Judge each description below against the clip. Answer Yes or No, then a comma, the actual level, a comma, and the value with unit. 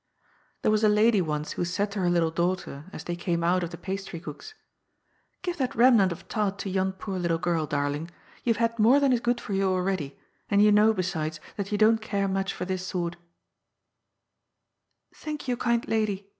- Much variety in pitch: No, average, 4.0 semitones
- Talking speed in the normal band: No, fast, 210 wpm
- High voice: Yes, high, 195 Hz